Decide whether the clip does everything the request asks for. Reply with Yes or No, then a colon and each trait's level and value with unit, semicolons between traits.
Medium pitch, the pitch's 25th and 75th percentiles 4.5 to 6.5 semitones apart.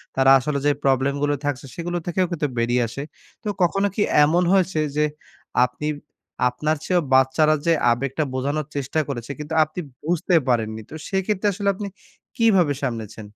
Yes: medium, 150 Hz; average, 4.8 semitones